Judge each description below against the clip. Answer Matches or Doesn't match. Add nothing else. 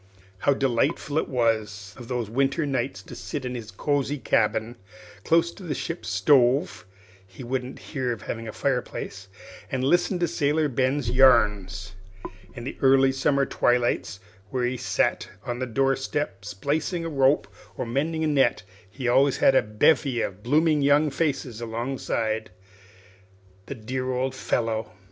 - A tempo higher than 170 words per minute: Doesn't match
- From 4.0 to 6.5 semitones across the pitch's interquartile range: Doesn't match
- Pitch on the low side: Matches